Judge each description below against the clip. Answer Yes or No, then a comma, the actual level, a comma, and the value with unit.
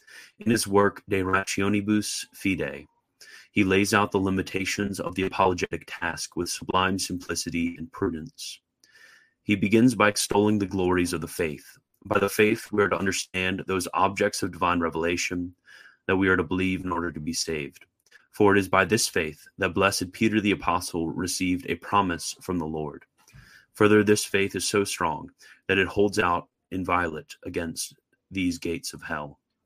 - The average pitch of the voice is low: Yes, very low, 95 Hz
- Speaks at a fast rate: No, average, 170 wpm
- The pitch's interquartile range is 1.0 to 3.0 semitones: Yes, narrow, 2.4 semitones